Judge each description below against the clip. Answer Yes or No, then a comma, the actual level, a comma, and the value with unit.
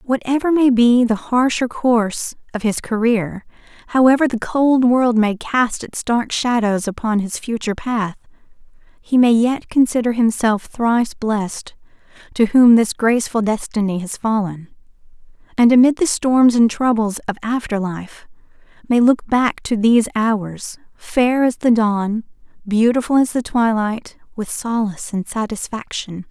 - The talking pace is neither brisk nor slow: Yes, average, 145 wpm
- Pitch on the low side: No, high, 230 Hz